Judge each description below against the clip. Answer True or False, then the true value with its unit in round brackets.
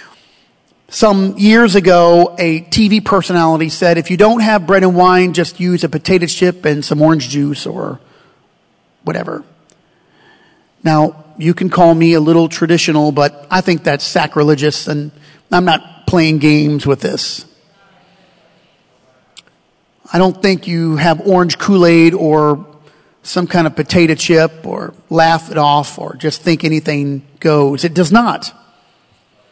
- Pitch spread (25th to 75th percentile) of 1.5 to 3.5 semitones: True (2.8 semitones)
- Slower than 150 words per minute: True (140 wpm)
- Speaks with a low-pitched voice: False (165 Hz)